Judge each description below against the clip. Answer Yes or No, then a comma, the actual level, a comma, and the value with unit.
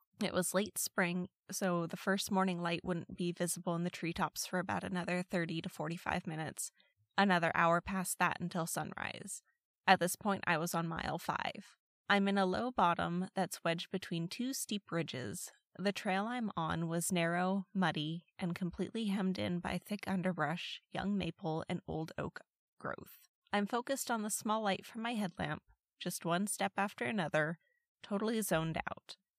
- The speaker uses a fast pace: No, average, 170 wpm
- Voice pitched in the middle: Yes, medium, 180 Hz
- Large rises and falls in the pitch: No, average, 2.7 semitones